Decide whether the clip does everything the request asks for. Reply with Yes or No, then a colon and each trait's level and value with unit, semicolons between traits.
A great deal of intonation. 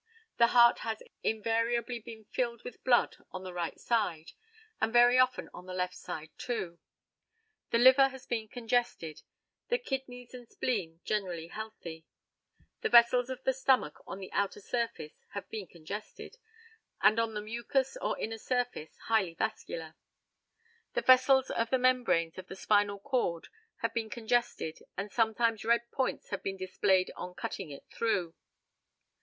No: average, 4.6 semitones